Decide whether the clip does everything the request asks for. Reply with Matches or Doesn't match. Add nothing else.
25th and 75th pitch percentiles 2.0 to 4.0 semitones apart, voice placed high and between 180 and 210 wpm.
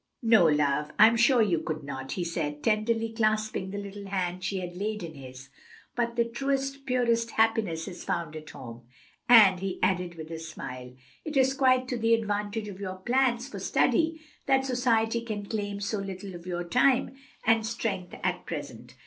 Doesn't match